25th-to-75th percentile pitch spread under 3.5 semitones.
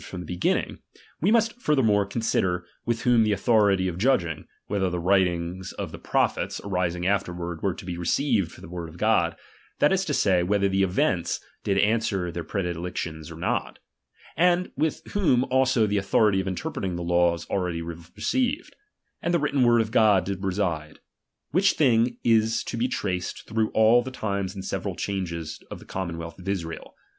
No: average, 4.8 semitones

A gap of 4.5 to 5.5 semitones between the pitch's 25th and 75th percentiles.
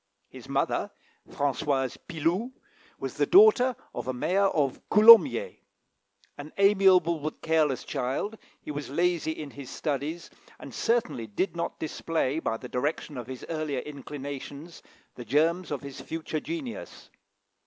Yes: average, 4.9 semitones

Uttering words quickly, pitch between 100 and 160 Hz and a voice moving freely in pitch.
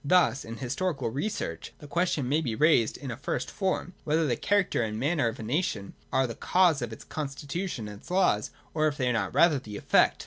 Yes: fast, 220 wpm; medium, 140 Hz; wide, 6.6 semitones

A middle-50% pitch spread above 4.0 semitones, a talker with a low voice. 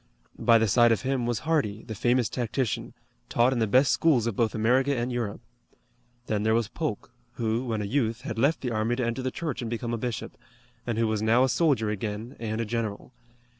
No: narrow, 2.5 semitones; low, 115 Hz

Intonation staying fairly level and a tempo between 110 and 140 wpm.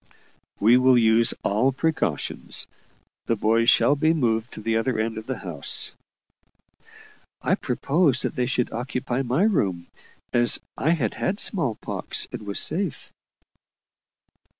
No: average, 3.8 semitones; slow, 135 wpm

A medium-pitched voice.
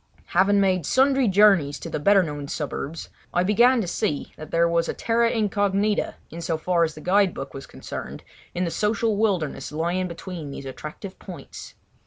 Yes: medium, 180 Hz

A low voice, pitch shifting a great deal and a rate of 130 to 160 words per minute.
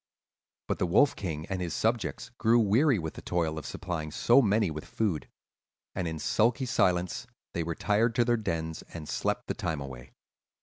No: very low, 90 Hz; wide, 5.8 semitones; average, 180 wpm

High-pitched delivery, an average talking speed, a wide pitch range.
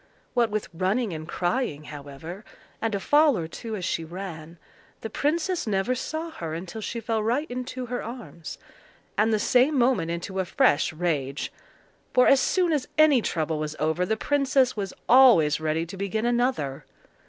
Yes: high, 210 Hz; average, 170 wpm; wide, 7.3 semitones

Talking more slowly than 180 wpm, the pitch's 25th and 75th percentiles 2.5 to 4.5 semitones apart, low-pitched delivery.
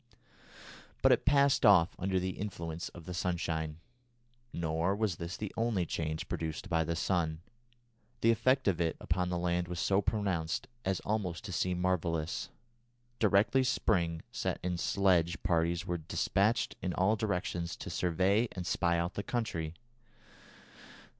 Yes: average, 150 wpm; average, 3.2 semitones; very low, 90 Hz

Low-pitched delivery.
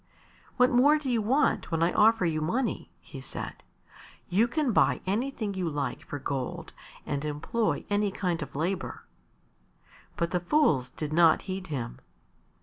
No: medium, 185 Hz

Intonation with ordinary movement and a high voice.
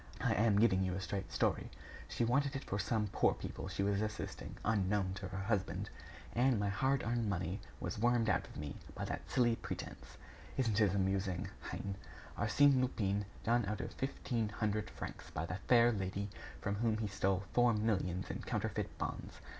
No: average, 3.3 semitones; low, 105 Hz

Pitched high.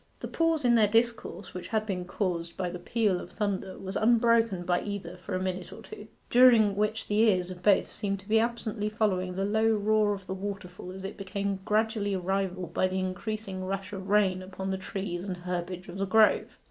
Yes: high, 195 Hz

